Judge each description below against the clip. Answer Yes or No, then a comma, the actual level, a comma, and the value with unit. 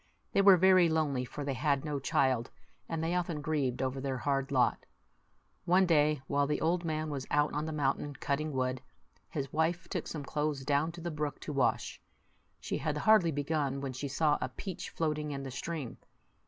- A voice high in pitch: No, medium, 150 Hz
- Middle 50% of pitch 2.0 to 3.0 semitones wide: Yes, average, 2.7 semitones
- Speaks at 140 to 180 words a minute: No, average, 195 wpm